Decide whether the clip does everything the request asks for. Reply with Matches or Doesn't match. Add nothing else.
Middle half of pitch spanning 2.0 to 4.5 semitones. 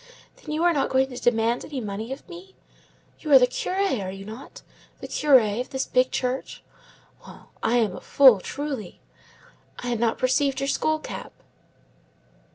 Matches